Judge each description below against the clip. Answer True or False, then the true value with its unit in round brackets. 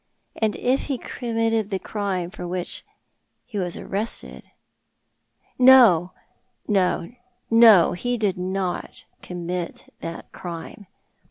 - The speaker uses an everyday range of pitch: True (4.1 semitones)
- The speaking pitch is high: True (195 Hz)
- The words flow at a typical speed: False (110 wpm)